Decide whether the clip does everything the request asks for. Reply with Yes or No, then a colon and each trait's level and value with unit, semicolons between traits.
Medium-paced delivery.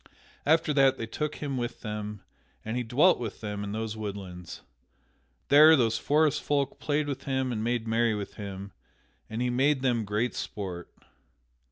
Yes: average, 170 wpm